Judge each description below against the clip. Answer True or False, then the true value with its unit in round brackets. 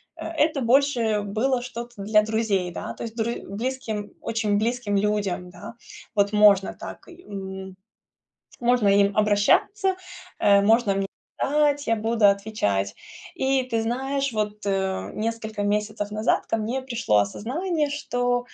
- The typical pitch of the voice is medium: False (220 Hz)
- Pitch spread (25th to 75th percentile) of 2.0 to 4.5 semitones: True (3.4 semitones)